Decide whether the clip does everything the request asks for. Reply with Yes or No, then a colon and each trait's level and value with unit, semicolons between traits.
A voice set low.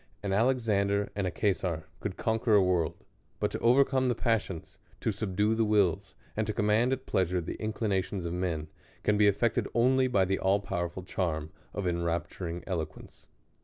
Yes: low, 100 Hz